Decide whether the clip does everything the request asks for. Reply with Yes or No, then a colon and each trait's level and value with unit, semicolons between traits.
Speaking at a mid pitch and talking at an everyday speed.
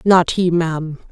Yes: medium, 170 Hz; average, 160 wpm